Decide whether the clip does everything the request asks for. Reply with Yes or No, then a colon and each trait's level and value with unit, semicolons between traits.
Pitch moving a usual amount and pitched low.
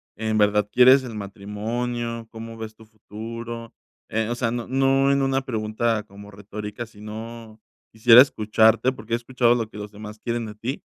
No: narrow, 1.9 semitones; low, 115 Hz